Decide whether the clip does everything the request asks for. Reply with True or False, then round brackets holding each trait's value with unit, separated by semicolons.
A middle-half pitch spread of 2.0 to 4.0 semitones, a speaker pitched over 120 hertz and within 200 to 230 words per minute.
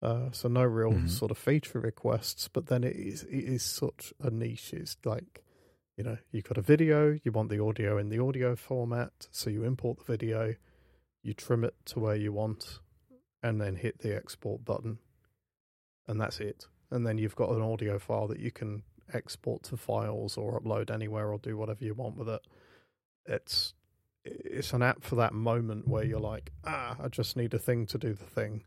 False (2.5 semitones; 115 Hz; 205 wpm)